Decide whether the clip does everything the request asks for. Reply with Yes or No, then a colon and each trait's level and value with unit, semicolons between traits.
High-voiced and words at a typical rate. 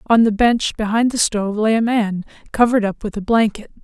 No: high, 220 Hz; fast, 220 wpm